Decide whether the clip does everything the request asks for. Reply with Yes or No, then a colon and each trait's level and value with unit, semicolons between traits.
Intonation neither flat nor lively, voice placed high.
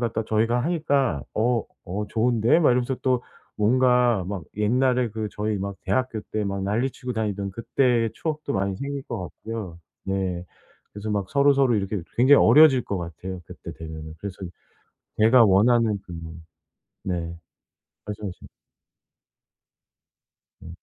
No: average, 4.3 semitones; low, 110 Hz